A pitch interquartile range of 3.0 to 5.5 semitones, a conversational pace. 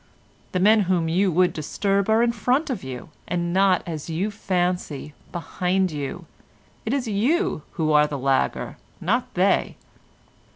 Yes: average, 4.5 semitones; average, 155 wpm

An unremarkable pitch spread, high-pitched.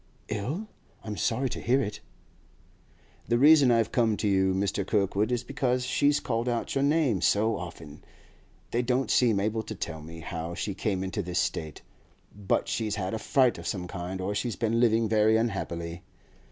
No: average, 4.3 semitones; low, 110 Hz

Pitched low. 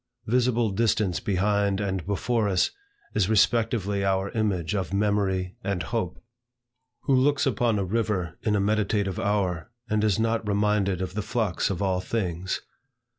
Yes: low, 100 Hz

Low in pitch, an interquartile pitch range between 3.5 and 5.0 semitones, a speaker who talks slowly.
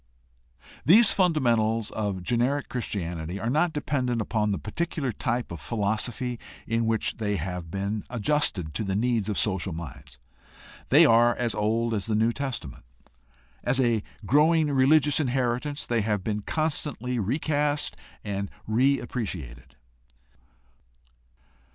Yes: low, 115 Hz; average, 4.6 semitones; slow, 130 wpm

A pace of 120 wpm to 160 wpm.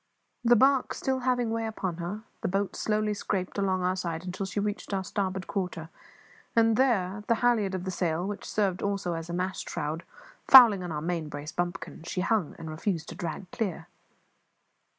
No: average, 185 wpm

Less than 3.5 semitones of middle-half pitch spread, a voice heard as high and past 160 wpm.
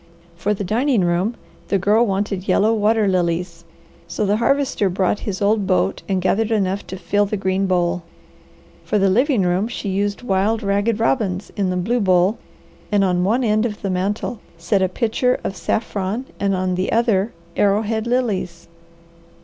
Yes: average, 2.9 semitones; high, 200 Hz; average, 175 wpm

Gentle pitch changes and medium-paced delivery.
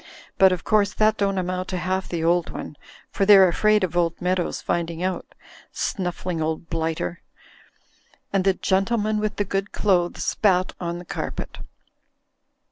Yes: narrow, 2.3 semitones; average, 155 wpm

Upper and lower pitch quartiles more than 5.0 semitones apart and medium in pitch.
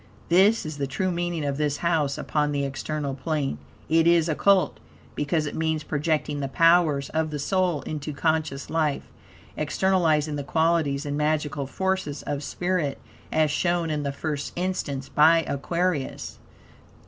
No: average, 2.8 semitones; medium, 155 Hz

